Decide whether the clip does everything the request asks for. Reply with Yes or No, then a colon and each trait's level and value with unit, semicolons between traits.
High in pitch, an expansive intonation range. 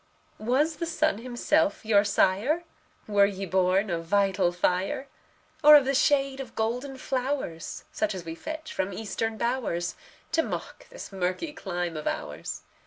Yes: high, 220 Hz; wide, 6.6 semitones